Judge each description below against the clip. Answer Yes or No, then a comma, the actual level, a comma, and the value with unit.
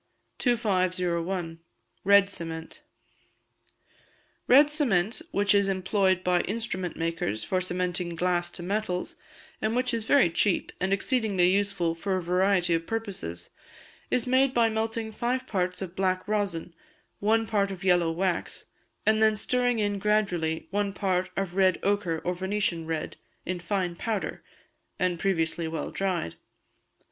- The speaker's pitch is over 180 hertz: Yes, high, 190 Hz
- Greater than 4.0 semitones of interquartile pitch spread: No, average, 3.2 semitones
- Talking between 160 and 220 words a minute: No, average, 140 wpm